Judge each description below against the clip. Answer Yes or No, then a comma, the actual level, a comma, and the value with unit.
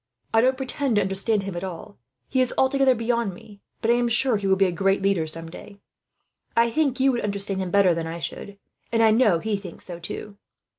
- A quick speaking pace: Yes, fast, 235 wpm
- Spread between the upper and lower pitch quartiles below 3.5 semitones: No, average, 3.8 semitones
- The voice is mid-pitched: No, high, 205 Hz